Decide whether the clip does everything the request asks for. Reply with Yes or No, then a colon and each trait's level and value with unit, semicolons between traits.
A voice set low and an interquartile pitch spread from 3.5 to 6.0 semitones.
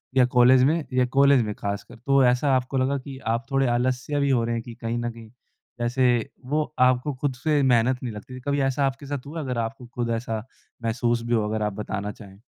No: low, 125 Hz; average, 2.8 semitones